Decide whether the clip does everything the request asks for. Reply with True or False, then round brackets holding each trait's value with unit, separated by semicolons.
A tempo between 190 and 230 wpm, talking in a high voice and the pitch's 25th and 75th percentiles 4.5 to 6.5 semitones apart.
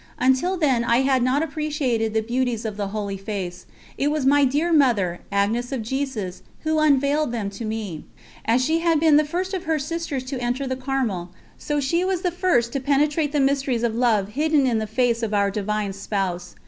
True (205 wpm; 255 Hz; 5.3 semitones)